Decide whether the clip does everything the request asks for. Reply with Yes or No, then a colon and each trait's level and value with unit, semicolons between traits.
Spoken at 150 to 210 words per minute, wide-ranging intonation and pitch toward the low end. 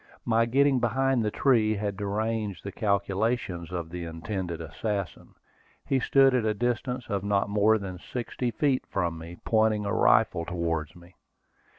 No: average, 160 wpm; average, 4.6 semitones; low, 105 Hz